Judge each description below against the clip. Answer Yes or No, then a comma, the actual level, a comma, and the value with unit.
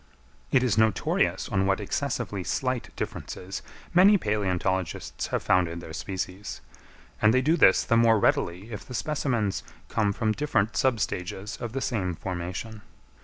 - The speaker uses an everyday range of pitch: Yes, average, 4.4 semitones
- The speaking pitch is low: Yes, low, 105 Hz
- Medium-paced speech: Yes, average, 150 wpm